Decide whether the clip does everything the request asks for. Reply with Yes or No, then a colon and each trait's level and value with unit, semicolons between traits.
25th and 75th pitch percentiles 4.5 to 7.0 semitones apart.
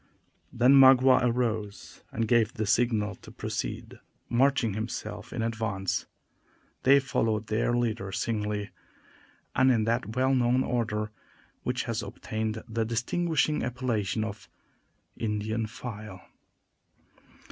No: narrow, 2.5 semitones